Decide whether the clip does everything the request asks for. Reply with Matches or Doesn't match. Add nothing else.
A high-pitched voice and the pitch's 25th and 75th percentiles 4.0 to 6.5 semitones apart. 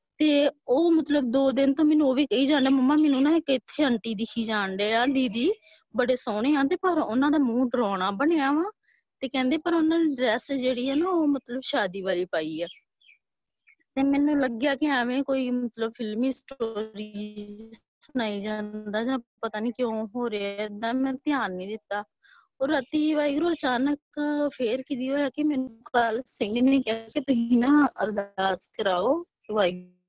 Matches